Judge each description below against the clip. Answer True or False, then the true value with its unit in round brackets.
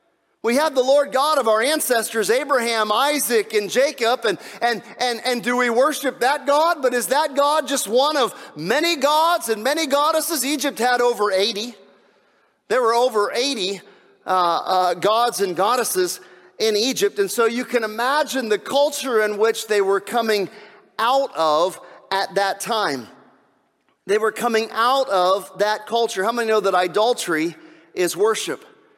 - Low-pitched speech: False (235 Hz)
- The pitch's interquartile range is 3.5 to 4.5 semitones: False (5.1 semitones)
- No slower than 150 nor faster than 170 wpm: True (165 wpm)